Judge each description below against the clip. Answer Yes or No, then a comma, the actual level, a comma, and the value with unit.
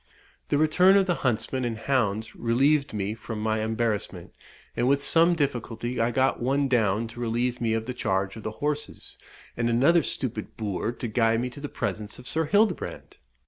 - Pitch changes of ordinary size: Yes, average, 4.0 semitones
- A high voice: No, low, 120 Hz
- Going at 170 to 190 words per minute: Yes, average, 185 wpm